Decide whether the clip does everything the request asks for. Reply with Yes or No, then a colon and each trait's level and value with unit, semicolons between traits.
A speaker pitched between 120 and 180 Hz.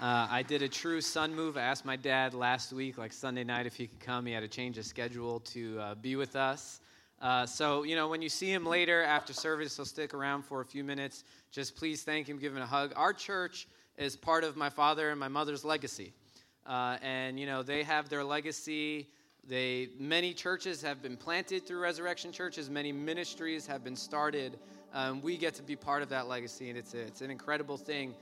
Yes: medium, 140 Hz